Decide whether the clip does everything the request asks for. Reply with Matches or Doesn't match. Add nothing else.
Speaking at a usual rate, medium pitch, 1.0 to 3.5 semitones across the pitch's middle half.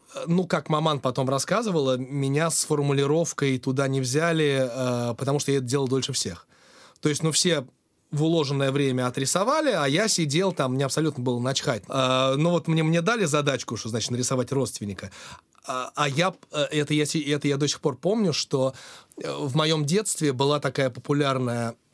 Doesn't match